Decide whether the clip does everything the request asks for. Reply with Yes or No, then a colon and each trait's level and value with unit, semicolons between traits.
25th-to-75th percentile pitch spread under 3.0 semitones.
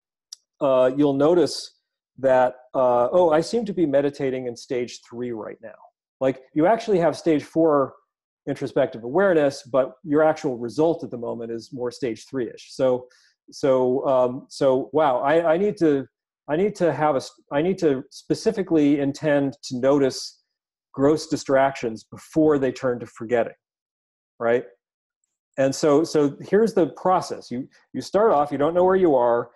No: average, 4.0 semitones